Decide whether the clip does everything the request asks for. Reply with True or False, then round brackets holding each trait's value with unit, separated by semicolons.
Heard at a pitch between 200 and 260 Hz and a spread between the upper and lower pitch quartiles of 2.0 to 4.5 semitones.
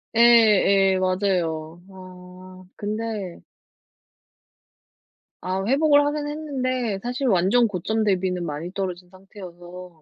False (190 Hz; 4.1 semitones)